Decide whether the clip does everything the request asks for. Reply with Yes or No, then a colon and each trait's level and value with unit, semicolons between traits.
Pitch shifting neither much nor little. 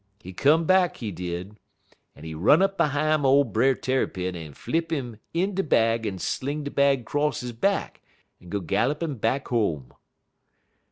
No: wide, 6.8 semitones